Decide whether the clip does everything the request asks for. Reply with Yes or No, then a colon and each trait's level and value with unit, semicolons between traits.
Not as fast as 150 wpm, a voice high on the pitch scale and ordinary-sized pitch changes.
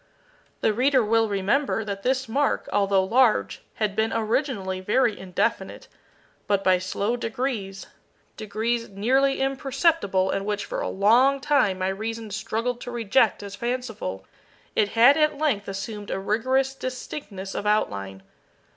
Yes: average, 140 wpm; high, 220 Hz; average, 4.6 semitones